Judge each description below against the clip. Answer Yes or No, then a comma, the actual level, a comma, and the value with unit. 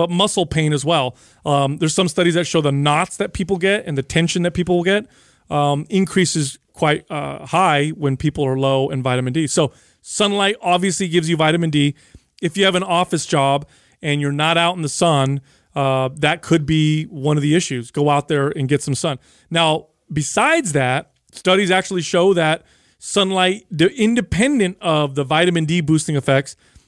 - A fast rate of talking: No, average, 190 wpm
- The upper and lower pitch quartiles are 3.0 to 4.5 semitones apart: Yes, average, 4.0 semitones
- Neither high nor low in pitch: Yes, medium, 160 Hz